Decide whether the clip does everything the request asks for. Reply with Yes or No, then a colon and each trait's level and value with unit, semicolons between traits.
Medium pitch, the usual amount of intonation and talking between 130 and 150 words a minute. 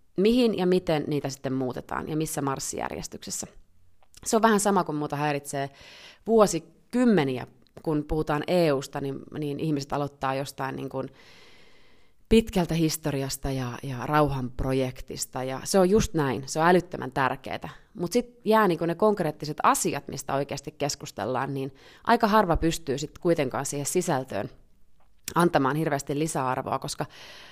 Yes: medium, 150 Hz; average, 4.0 semitones; average, 135 wpm